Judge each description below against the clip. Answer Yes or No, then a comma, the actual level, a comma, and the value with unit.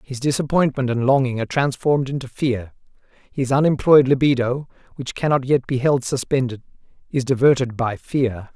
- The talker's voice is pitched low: Yes, low, 130 Hz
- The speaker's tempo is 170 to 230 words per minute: No, average, 145 wpm